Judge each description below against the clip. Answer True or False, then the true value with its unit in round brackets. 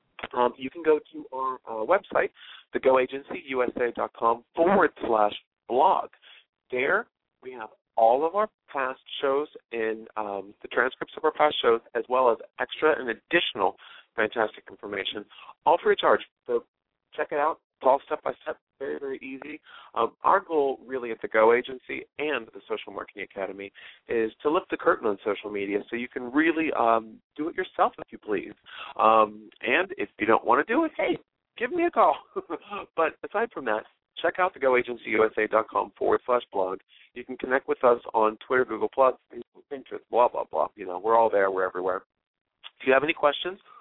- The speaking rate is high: False (185 wpm)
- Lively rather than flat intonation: True (7.0 semitones)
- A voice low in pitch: True (130 Hz)